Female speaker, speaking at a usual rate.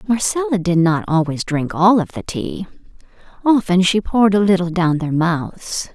Yes: female; average, 170 wpm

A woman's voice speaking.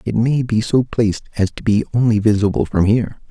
No: male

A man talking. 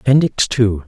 Yes: male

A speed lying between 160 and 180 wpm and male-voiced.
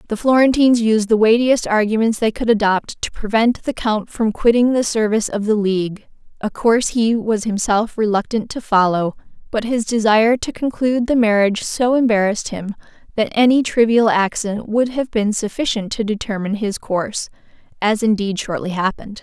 No: average, 170 wpm; female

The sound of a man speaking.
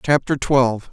Yes: male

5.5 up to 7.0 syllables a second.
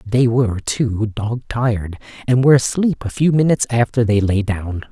No: 5.1 syllables/s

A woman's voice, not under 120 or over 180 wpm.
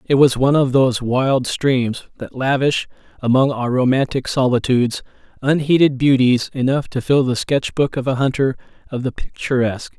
No: male; average, 160 wpm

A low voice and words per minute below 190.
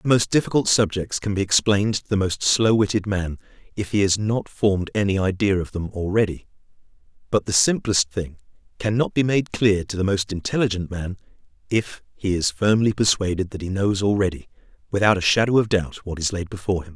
No: low, 100 Hz; average, 195 wpm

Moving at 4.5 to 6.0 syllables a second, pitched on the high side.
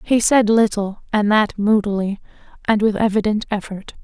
Yes: 4.9 syllables/s; high, 210 Hz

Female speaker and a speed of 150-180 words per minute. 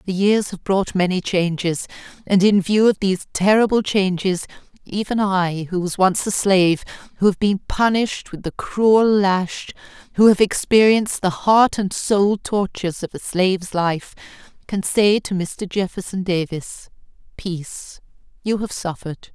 Yes: female; average, 155 wpm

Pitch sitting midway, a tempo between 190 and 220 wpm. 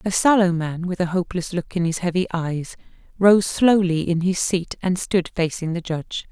Yes: medium, 175 Hz; average, 200 wpm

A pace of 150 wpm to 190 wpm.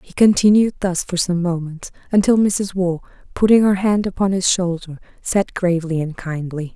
Yes: average, 170 wpm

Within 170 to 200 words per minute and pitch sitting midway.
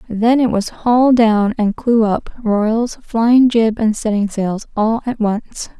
No: average, 175 wpm; high, 225 Hz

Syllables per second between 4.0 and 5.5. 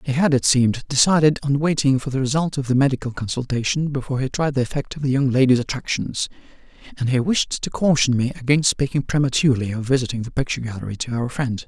No: 6.5 syllables/s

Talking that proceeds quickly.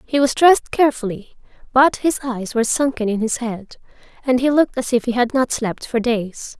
Yes: fast, 210 wpm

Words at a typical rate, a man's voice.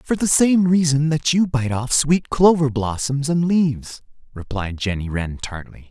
Yes: average, 175 wpm; male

